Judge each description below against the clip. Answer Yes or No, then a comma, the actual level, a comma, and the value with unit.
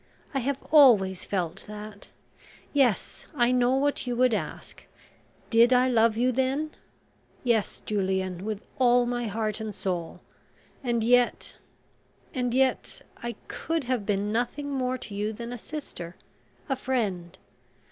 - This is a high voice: Yes, high, 240 Hz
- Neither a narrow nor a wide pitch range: Yes, average, 3.6 semitones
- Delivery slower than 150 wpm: Yes, average, 140 wpm